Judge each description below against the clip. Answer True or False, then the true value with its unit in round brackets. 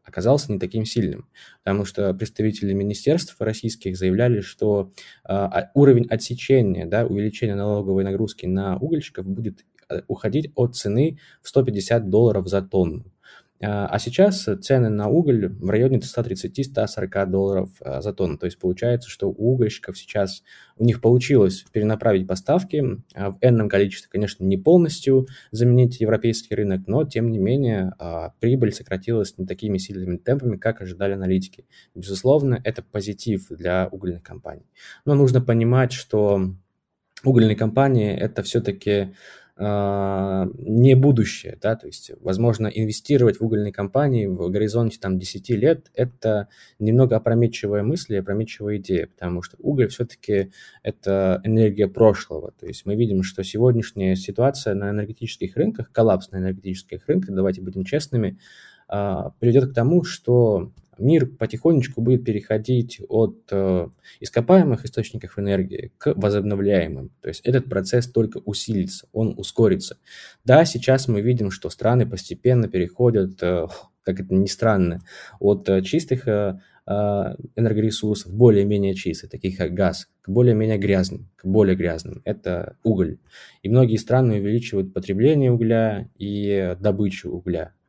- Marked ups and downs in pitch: False (3.7 semitones)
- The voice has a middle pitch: False (105 Hz)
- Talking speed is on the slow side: False (135 wpm)